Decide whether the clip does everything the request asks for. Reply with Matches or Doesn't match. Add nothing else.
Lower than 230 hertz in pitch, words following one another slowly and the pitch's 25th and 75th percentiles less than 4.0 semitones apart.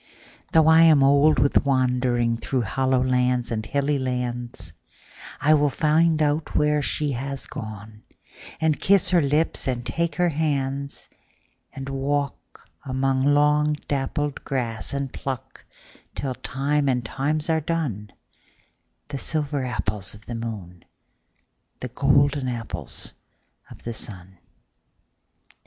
Matches